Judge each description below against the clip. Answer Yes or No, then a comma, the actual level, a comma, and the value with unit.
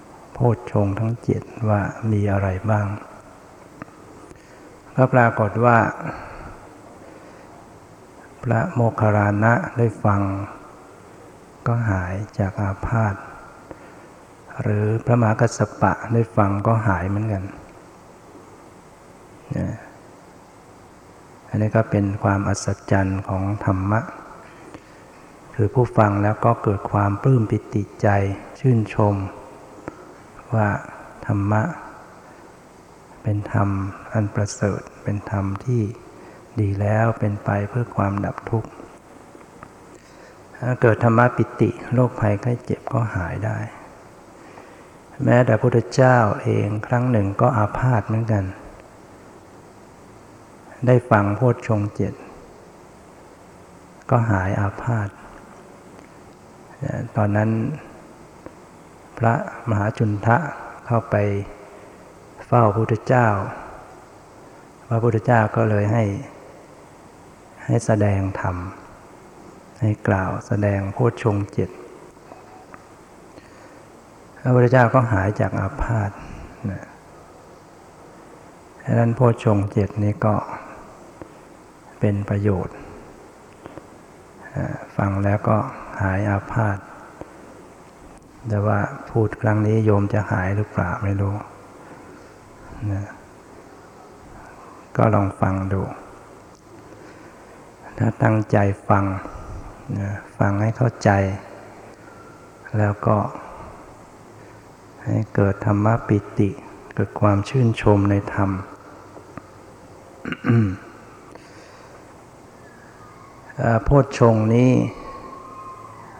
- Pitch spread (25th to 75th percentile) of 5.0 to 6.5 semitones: No, narrow, 2.5 semitones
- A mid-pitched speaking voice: No, low, 105 Hz